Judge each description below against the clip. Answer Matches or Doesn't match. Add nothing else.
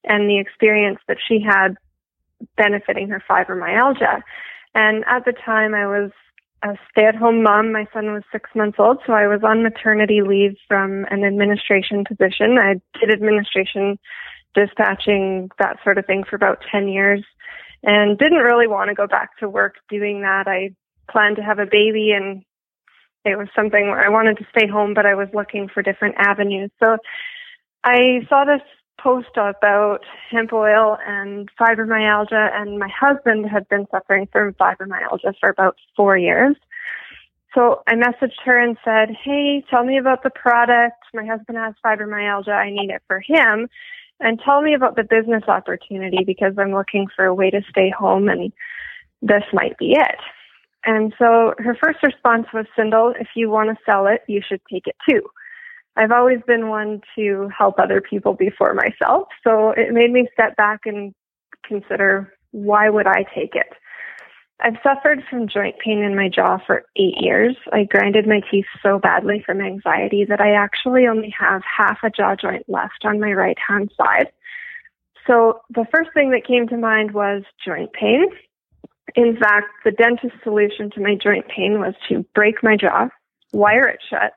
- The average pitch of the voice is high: Matches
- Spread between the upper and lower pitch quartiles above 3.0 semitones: Doesn't match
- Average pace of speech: Matches